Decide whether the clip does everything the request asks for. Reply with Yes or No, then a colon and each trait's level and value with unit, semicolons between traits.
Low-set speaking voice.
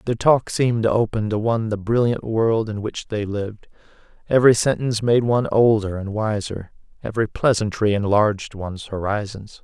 Yes: low, 110 Hz